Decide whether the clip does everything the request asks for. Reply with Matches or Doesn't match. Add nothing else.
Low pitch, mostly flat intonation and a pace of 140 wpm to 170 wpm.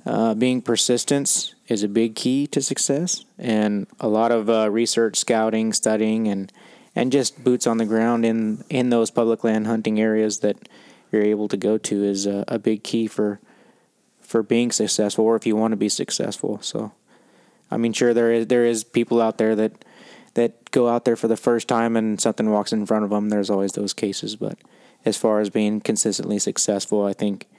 Doesn't match